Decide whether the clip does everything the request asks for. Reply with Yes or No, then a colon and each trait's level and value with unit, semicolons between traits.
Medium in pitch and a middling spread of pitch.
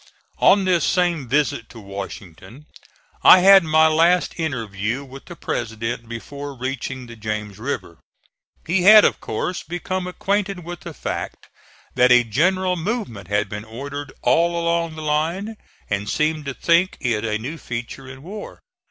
No: medium, 145 Hz; wide, 7.1 semitones